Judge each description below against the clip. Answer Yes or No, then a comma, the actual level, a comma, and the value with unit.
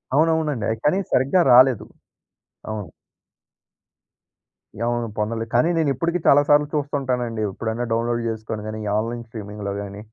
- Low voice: Yes, low, 120 Hz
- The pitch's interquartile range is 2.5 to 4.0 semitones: No, average, 4.6 semitones